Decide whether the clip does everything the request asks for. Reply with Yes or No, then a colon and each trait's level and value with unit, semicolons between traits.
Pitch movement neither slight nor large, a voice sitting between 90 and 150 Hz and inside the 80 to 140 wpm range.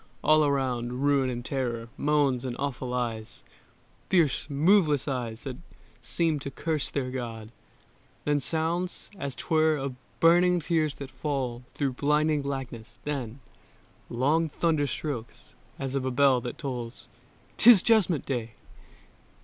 Yes: average, 3.7 semitones; medium, 140 Hz; slow, 135 wpm